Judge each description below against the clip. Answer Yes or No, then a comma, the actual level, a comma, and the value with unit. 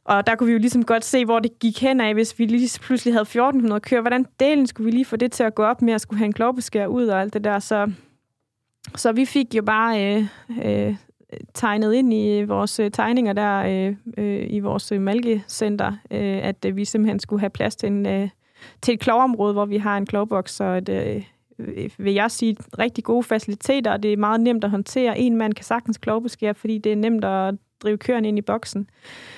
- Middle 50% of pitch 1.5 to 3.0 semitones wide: Yes, narrow, 2.4 semitones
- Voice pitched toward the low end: No, high, 215 Hz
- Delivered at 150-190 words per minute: No, fast, 225 wpm